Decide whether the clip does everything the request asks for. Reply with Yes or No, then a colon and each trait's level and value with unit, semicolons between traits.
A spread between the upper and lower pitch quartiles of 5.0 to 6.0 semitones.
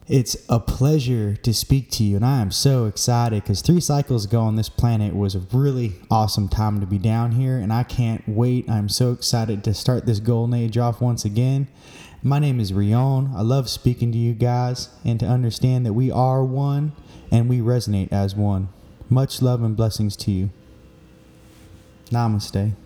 No: average, 3.0 semitones